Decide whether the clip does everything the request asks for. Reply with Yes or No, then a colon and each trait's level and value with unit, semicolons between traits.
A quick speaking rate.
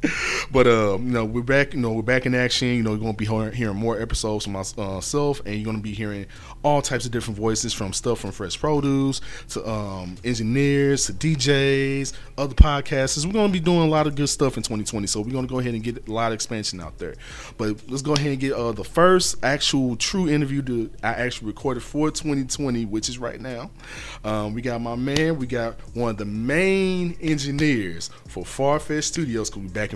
Yes: fast, 220 wpm